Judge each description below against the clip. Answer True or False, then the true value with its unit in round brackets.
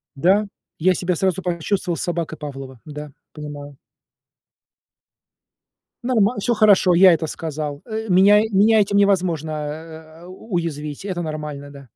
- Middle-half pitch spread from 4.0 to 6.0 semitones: True (4.6 semitones)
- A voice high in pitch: False (170 Hz)